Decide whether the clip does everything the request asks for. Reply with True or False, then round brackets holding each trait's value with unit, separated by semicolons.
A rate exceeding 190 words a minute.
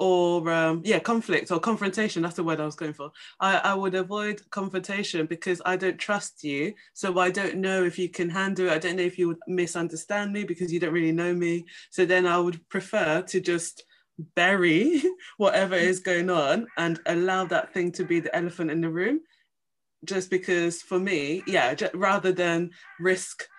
True (200 wpm)